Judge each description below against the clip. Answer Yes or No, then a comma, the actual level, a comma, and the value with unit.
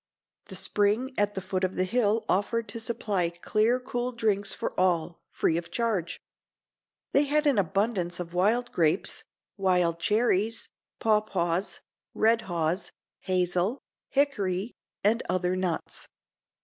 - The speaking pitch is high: Yes, high, 200 Hz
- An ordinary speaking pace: No, slow, 130 wpm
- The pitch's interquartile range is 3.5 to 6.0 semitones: Yes, average, 4.2 semitones